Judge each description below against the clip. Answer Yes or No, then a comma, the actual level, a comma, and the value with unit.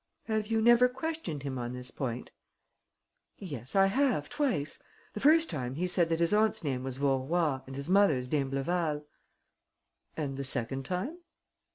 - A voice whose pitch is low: No, medium, 155 Hz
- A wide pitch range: Yes, wide, 7.7 semitones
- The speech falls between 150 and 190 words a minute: Yes, average, 160 wpm